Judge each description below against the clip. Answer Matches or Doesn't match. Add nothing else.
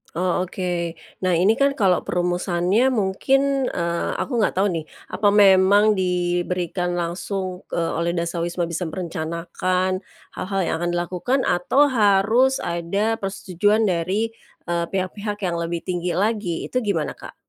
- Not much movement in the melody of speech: Doesn't match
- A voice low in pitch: Doesn't match